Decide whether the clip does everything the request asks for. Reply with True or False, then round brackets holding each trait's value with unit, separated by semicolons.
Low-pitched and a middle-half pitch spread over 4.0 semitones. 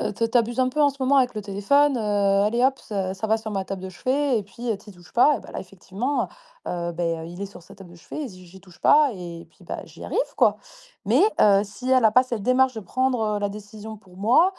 False (215 Hz; 4.9 semitones)